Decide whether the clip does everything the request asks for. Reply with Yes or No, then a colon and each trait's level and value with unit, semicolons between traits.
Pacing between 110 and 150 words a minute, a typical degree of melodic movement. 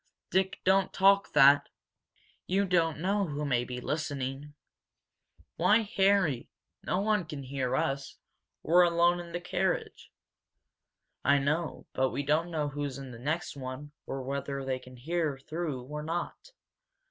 Yes: average, 145 wpm; average, 4.4 semitones